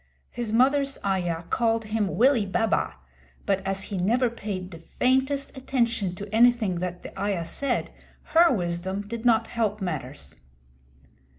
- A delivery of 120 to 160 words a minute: Yes, average, 140 wpm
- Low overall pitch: No, high, 215 Hz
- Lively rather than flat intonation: No, average, 4.4 semitones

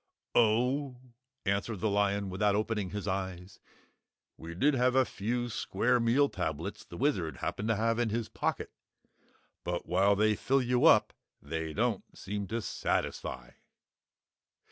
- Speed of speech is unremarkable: Yes, average, 145 wpm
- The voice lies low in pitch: Yes, low, 105 Hz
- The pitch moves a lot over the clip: No, average, 3.7 semitones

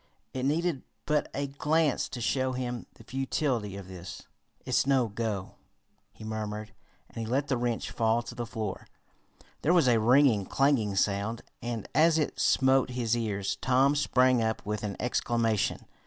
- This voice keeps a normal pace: Yes, average, 165 wpm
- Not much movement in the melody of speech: No, average, 3.6 semitones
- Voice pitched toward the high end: No, low, 120 Hz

